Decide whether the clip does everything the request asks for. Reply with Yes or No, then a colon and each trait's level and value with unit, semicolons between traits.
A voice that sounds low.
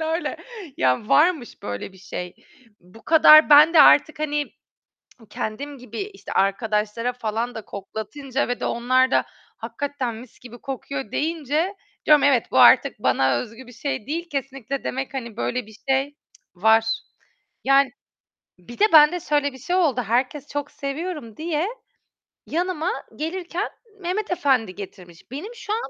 No: very high, 270 Hz